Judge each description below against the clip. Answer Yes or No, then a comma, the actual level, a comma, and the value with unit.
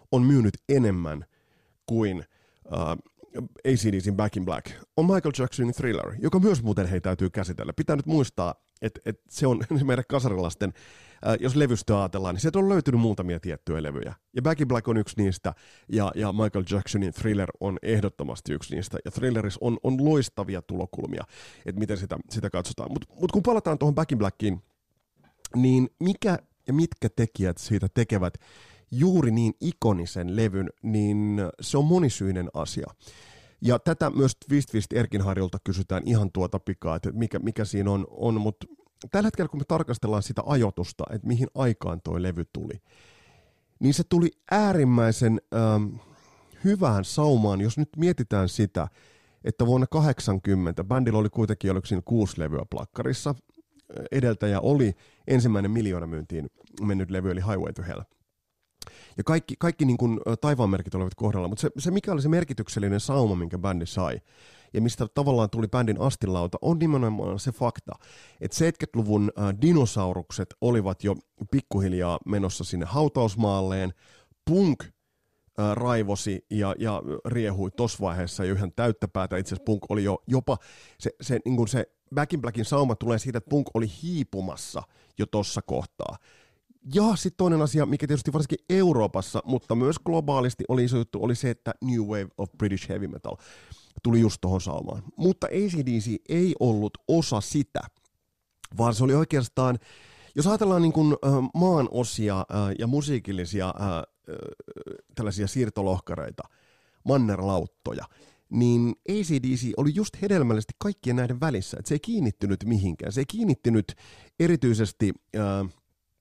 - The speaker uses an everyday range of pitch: No, wide, 5.7 semitones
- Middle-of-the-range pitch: No, low, 110 Hz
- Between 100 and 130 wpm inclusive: No, average, 150 wpm